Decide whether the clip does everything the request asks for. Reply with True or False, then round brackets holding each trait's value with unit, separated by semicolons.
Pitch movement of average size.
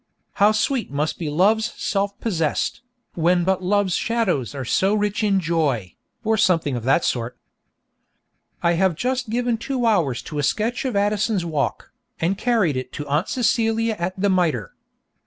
False (5.9 semitones)